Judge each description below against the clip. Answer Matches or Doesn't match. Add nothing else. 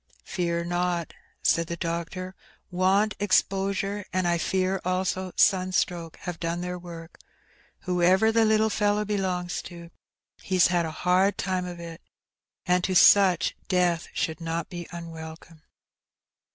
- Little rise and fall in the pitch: Matches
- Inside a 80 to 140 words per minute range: Matches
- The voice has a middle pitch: Matches